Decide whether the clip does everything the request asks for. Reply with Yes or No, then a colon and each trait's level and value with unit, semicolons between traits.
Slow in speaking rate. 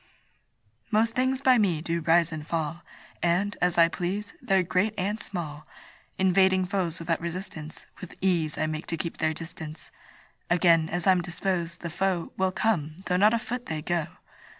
No: average, 175 wpm